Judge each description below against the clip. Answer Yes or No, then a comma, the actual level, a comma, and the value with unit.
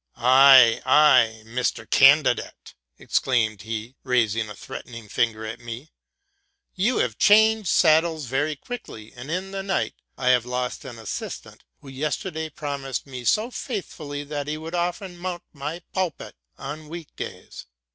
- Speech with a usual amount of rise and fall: No, wide, 6.0 semitones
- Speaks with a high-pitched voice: No, medium, 145 Hz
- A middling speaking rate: Yes, average, 155 wpm